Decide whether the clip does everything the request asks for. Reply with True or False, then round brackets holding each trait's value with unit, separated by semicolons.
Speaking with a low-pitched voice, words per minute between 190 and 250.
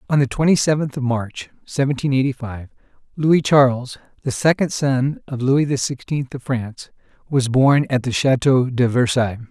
False (130 Hz; 170 wpm)